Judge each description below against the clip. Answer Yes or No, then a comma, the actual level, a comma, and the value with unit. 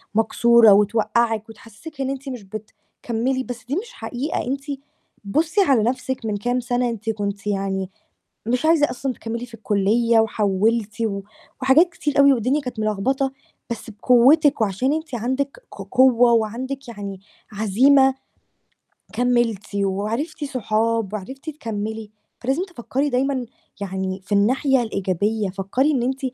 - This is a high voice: Yes, high, 235 Hz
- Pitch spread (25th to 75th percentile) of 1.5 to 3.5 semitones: No, average, 4.0 semitones